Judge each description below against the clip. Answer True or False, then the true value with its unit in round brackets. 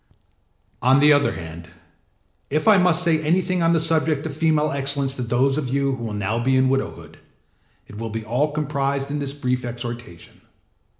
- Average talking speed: True (185 wpm)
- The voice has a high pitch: False (140 Hz)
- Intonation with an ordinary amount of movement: True (4.0 semitones)